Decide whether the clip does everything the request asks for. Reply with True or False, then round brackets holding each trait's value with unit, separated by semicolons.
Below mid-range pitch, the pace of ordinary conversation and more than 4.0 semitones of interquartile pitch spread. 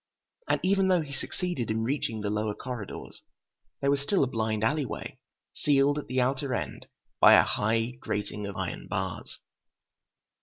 True (125 Hz; 165 wpm; 4.9 semitones)